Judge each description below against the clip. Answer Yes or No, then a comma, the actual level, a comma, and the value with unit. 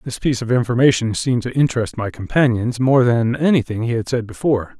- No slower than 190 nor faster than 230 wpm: Yes, average, 200 wpm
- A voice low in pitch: Yes, low, 120 Hz